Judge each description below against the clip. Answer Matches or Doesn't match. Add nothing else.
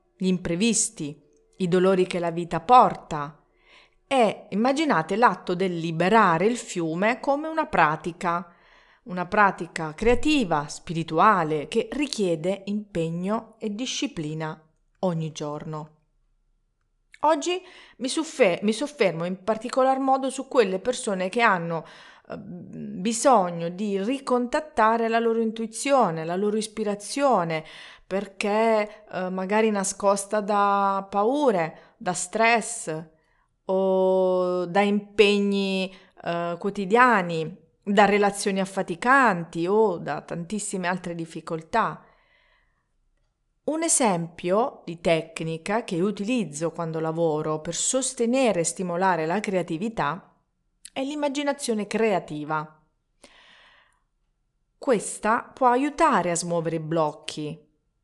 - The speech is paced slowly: Matches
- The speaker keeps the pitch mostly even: Doesn't match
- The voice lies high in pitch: Matches